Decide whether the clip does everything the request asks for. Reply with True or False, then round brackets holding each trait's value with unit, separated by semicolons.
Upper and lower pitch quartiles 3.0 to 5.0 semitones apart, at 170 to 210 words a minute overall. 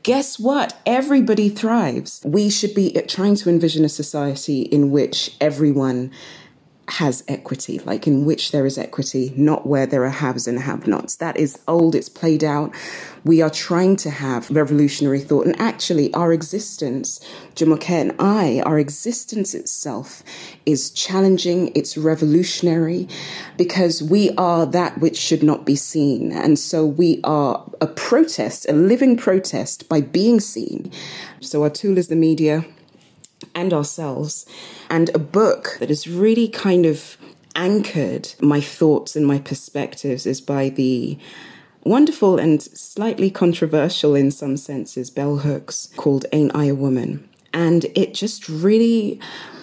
False (4.5 semitones; 150 wpm)